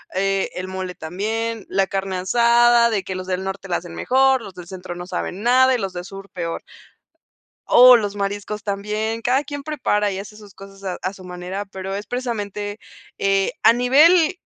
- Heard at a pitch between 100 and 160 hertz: No, high, 200 Hz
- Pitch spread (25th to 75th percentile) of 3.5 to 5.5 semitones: Yes, average, 3.8 semitones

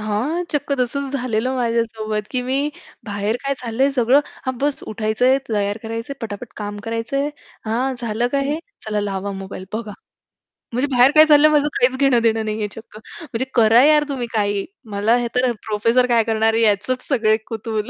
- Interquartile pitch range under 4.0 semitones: Yes, average, 3.2 semitones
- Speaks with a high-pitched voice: Yes, high, 230 Hz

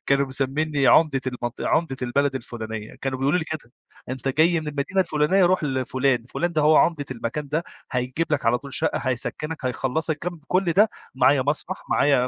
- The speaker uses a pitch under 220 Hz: Yes, medium, 140 Hz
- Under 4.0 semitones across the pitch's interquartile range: Yes, average, 3.5 semitones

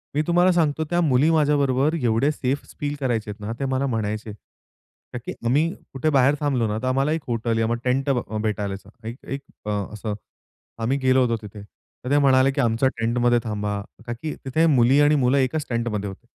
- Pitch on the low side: Yes, low, 130 Hz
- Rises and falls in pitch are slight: No, average, 3.9 semitones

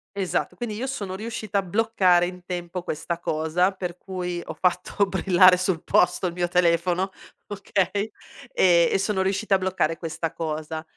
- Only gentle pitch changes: Yes, narrow, 2.0 semitones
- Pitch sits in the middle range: Yes, medium, 180 Hz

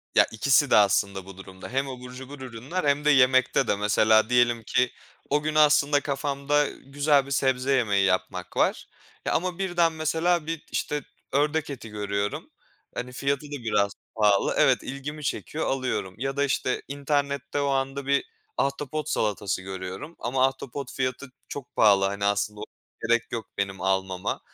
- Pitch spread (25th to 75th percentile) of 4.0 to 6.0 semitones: Yes, average, 5.2 semitones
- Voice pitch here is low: Yes, low, 130 Hz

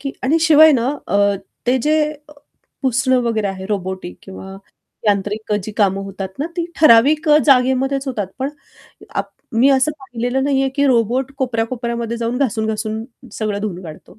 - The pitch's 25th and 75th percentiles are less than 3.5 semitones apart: No, average, 4.2 semitones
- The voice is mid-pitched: No, high, 235 Hz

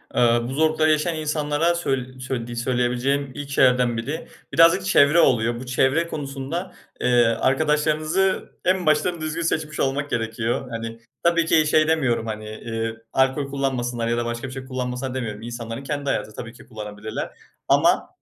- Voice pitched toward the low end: Yes, low, 130 Hz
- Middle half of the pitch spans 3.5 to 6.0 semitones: Yes, average, 4.4 semitones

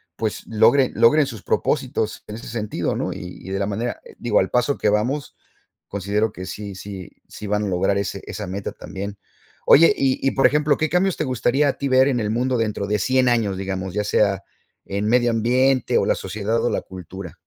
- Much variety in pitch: No, average, 4.4 semitones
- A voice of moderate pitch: No, low, 110 Hz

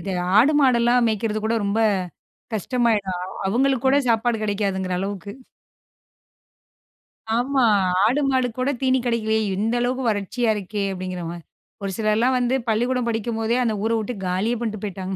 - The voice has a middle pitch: No, high, 225 Hz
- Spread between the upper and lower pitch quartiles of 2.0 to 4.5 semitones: Yes, average, 3.4 semitones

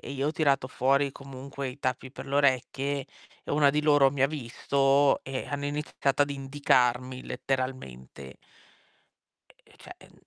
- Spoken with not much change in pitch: Yes, narrow, 1.6 semitones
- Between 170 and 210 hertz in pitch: No, low, 135 Hz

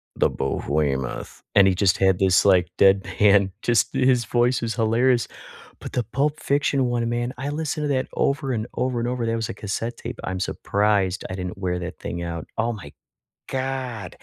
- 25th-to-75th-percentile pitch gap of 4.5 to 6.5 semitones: Yes, average, 4.8 semitones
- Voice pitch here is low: Yes, low, 115 Hz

